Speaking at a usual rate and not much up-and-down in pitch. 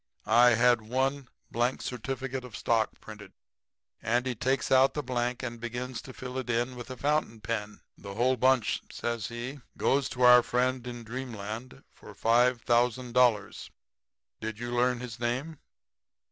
Yes: average, 150 wpm; narrow, 1.7 semitones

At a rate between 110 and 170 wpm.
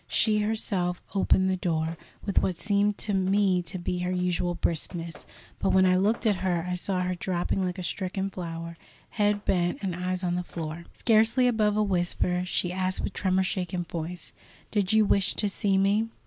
No: average, 190 wpm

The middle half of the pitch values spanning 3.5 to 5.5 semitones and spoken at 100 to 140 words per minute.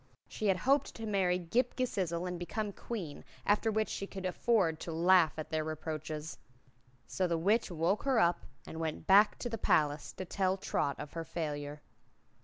No: average, 4.5 semitones; average, 185 wpm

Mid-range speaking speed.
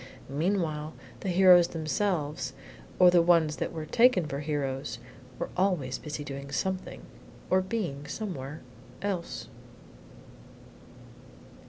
No: slow, 110 wpm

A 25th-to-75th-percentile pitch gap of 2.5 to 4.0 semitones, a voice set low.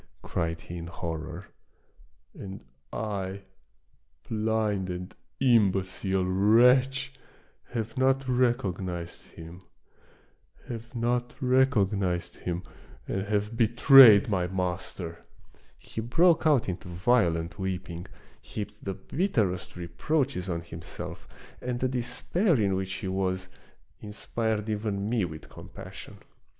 No: average, 4.8 semitones; low, 100 Hz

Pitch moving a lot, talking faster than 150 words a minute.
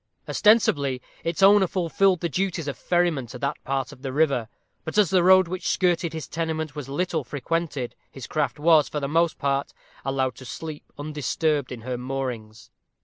No: average, 4.1 semitones; average, 180 wpm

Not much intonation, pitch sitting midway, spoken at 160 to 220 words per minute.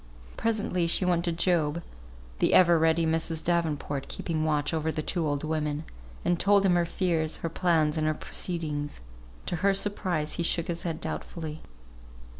Yes: narrow, 2.0 semitones; medium, 165 Hz; average, 170 wpm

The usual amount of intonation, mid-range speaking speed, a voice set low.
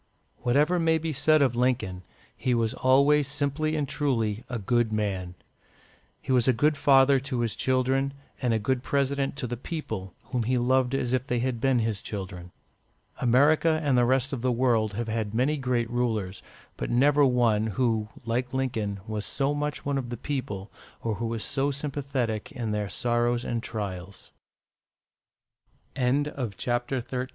Yes: average, 3.4 semitones; average, 165 wpm; low, 125 Hz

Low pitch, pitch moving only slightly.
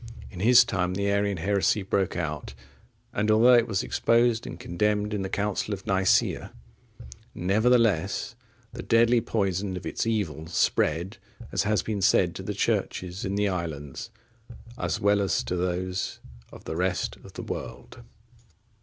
No: low, 100 Hz; average, 3.0 semitones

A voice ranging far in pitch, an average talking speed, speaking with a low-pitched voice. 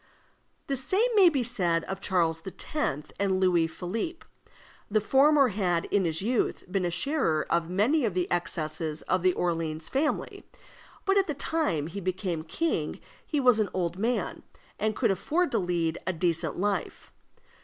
No: wide, 7.5 semitones; average, 165 wpm; high, 190 Hz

